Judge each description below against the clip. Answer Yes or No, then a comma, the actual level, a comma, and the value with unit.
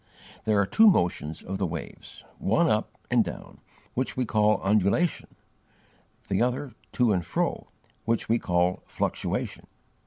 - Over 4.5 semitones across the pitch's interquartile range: Yes, average, 5.0 semitones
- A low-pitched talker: Yes, low, 105 Hz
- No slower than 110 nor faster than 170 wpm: Yes, average, 145 wpm